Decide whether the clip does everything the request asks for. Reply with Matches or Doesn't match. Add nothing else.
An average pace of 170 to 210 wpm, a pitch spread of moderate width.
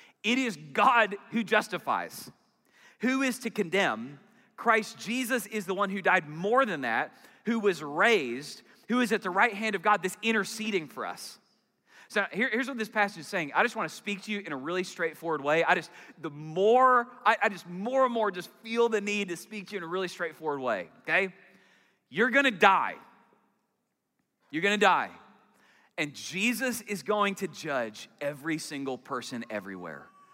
Matches